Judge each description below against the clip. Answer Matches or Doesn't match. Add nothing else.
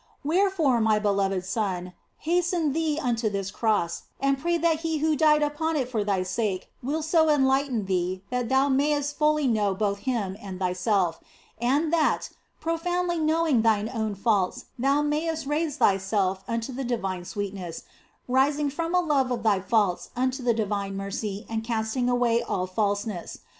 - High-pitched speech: Matches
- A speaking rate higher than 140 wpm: Matches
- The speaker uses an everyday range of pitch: Doesn't match